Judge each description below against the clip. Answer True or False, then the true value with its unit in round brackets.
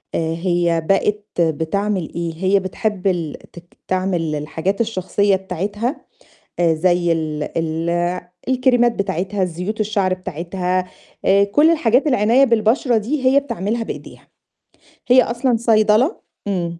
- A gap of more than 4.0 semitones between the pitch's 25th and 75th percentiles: True (4.6 semitones)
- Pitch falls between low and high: False (195 Hz)